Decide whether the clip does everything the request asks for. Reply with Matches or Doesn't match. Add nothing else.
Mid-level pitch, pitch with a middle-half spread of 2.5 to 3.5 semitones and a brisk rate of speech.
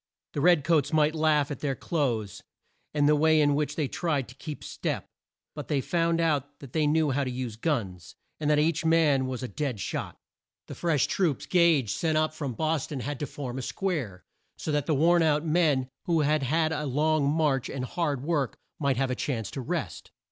Matches